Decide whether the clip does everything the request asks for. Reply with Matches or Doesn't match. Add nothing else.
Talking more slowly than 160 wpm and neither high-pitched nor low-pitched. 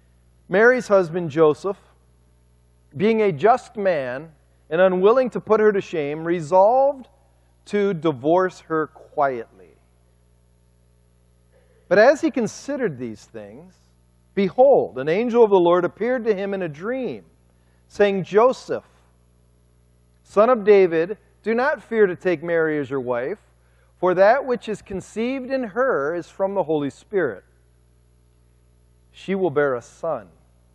Matches